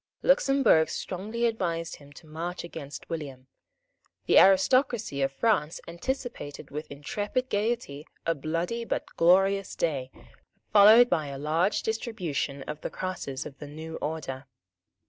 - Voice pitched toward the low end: No, medium, 165 Hz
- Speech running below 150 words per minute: Yes, slow, 135 wpm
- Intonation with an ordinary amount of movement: No, wide, 6.5 semitones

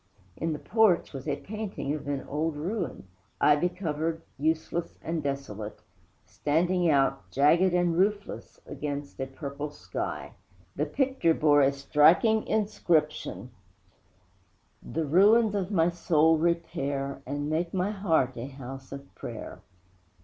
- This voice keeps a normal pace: No, slow, 130 wpm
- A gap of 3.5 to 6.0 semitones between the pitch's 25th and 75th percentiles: Yes, average, 4.0 semitones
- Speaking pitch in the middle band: Yes, medium, 155 Hz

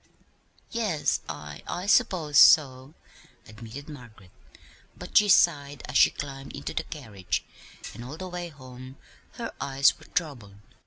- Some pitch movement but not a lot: Yes, average, 4.4 semitones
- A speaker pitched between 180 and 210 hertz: No, medium, 140 Hz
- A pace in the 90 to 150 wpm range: Yes, average, 140 wpm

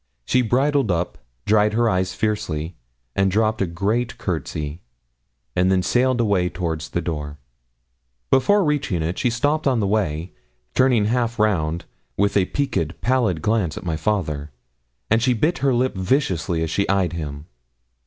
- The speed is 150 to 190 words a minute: Yes, average, 160 wpm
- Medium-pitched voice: No, low, 100 Hz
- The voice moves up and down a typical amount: No, wide, 6.0 semitones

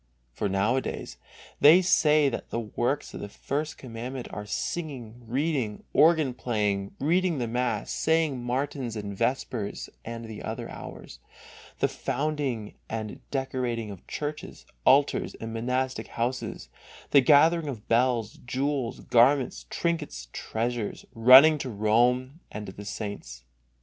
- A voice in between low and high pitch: No, low, 125 Hz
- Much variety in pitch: No, average, 4.3 semitones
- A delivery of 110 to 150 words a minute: Yes, slow, 135 wpm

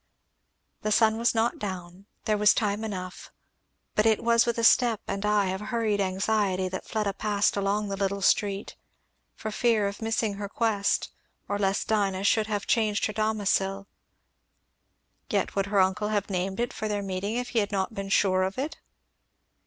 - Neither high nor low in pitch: No, high, 205 Hz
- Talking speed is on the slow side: No, average, 180 wpm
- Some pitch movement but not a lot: No, narrow, 1.9 semitones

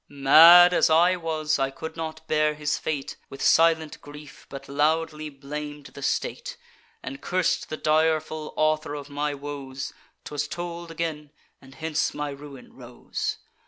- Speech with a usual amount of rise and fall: No, narrow, 1.9 semitones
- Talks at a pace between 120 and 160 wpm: Yes, average, 150 wpm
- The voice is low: No, medium, 155 Hz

